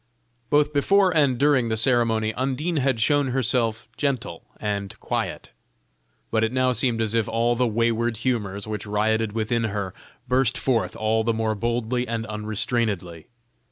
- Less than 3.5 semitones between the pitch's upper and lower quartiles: Yes, average, 2.8 semitones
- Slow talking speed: No, average, 155 wpm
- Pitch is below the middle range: Yes, low, 115 Hz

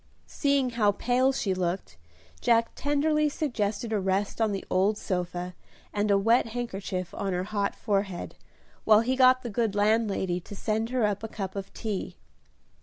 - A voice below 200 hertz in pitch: No, high, 210 Hz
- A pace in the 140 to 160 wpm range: No, average, 170 wpm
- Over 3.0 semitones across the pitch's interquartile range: Yes, average, 3.6 semitones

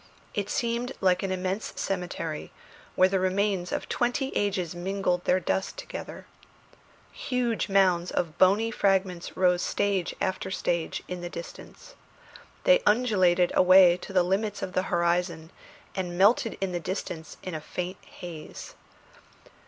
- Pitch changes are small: Yes, narrow, 2.2 semitones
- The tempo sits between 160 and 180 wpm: No, average, 140 wpm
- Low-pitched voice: No, medium, 185 Hz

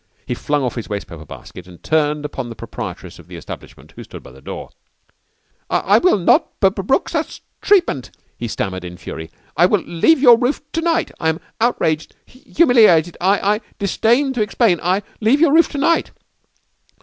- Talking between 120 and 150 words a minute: No, average, 175 wpm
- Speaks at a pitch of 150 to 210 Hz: Yes, high, 190 Hz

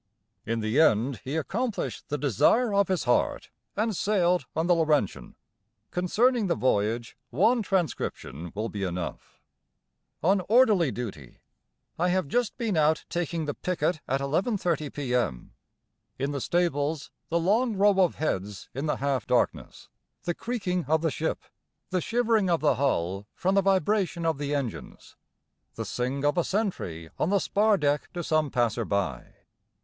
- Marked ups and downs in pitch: Yes, wide, 6.9 semitones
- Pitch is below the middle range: No, medium, 160 Hz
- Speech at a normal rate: Yes, average, 155 wpm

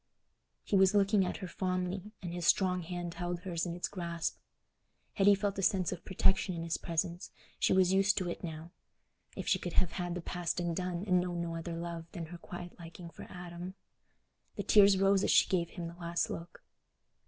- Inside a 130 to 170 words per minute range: No, average, 200 wpm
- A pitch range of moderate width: No, narrow, 1.7 semitones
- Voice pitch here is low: No, medium, 175 Hz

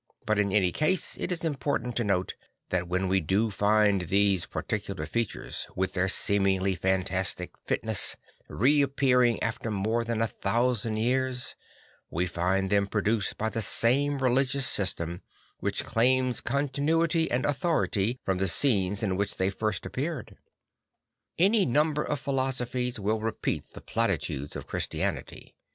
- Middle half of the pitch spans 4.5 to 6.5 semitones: Yes, average, 5.1 semitones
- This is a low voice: Yes, low, 110 Hz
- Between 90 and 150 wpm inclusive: Yes, average, 140 wpm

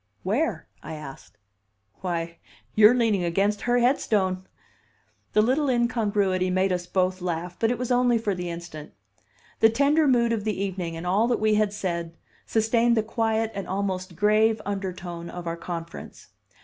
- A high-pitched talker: Yes, high, 200 Hz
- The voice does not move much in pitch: No, average, 4.1 semitones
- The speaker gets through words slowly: No, average, 160 wpm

